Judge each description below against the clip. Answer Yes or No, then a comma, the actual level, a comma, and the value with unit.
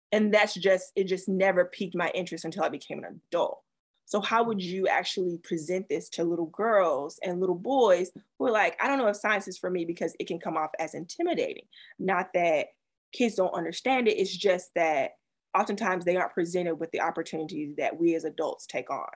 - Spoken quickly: Yes, fast, 210 wpm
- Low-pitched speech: No, medium, 185 Hz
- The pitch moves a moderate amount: Yes, average, 3.7 semitones